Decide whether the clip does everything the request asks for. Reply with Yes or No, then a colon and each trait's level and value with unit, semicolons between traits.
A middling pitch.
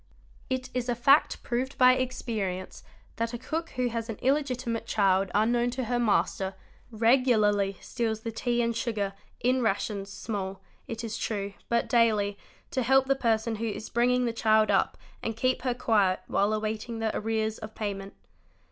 No: high, 230 Hz